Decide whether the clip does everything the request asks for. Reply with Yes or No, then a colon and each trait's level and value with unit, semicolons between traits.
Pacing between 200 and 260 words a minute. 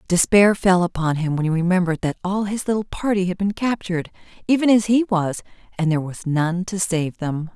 Yes: fast, 205 wpm